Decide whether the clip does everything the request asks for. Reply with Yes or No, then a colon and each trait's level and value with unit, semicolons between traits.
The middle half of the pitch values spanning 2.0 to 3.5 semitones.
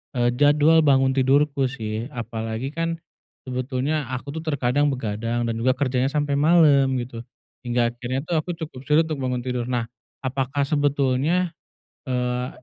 Yes: average, 2.9 semitones